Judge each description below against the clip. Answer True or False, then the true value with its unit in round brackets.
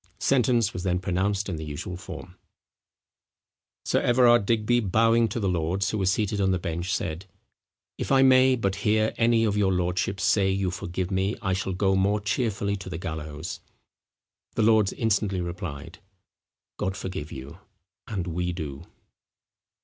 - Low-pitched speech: True (95 Hz)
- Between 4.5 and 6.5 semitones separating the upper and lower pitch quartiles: False (3.3 semitones)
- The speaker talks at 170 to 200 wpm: False (160 wpm)